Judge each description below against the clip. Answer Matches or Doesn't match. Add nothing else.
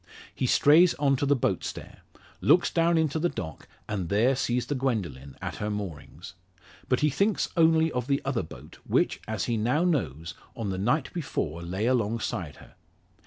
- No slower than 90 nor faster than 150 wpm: Doesn't match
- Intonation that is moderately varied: Doesn't match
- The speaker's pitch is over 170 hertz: Doesn't match